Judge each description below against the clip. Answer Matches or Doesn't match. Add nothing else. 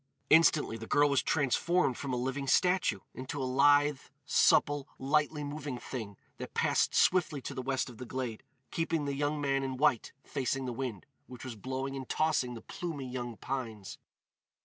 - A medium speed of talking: Matches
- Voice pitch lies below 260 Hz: Matches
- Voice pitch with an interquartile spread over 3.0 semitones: Doesn't match